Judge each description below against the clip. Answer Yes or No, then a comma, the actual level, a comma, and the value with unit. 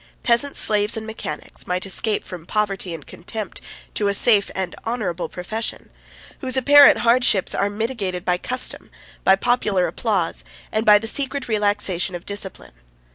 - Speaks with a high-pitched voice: Yes, high, 210 Hz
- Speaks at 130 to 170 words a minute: Yes, average, 150 wpm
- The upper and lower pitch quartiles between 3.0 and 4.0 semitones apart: Yes, average, 3.7 semitones